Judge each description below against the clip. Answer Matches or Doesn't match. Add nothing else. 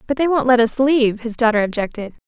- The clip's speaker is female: Matches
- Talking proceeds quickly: Matches